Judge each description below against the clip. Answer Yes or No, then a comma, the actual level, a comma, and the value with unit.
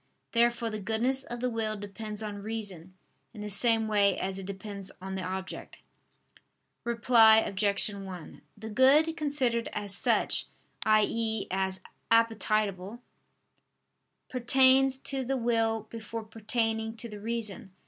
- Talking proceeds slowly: Yes, slow, 130 wpm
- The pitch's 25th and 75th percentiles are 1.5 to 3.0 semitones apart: Yes, average, 2.7 semitones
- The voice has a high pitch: Yes, high, 220 Hz